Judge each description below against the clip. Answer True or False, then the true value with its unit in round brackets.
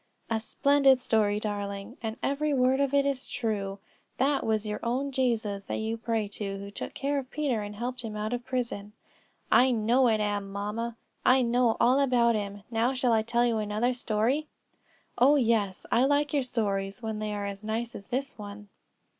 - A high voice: True (230 Hz)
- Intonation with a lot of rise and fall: False (3.5 semitones)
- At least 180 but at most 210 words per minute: True (195 wpm)